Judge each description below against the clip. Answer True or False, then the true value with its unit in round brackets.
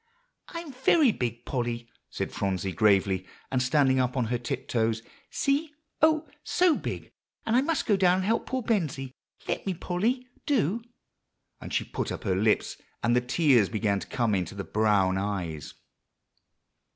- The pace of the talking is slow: False (165 wpm)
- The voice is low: True (125 Hz)